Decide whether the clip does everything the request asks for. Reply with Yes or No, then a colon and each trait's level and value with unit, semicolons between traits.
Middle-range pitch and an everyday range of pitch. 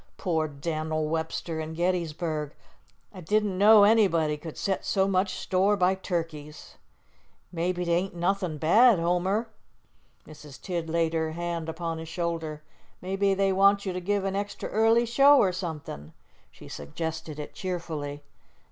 Yes: medium, 175 Hz; average, 3.4 semitones